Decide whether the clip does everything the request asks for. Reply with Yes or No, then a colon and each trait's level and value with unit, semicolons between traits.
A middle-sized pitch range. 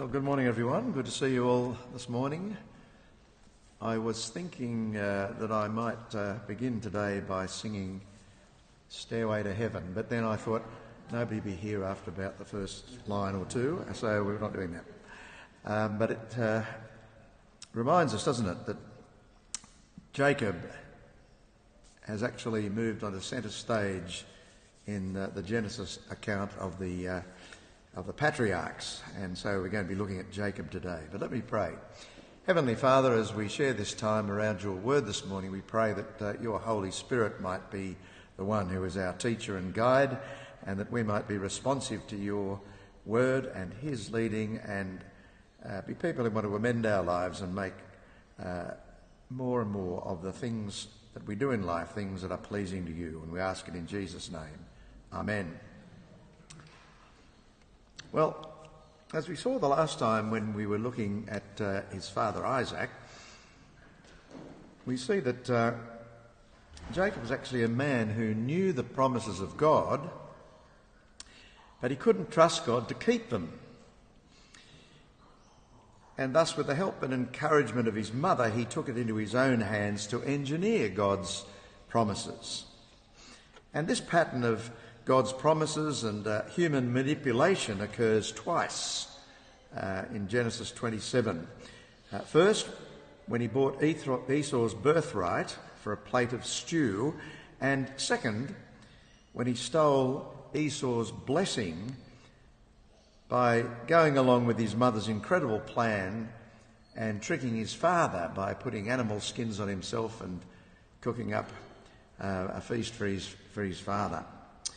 Yes: average, 3.8 semitones